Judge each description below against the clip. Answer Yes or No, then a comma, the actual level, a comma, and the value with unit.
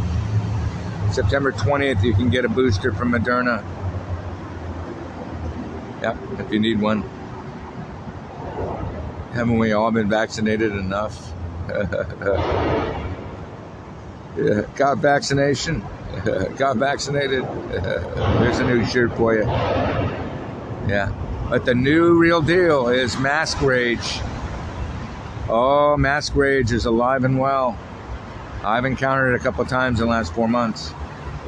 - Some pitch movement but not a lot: Yes, average, 4.7 semitones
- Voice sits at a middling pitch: No, low, 115 Hz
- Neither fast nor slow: No, slow, 110 wpm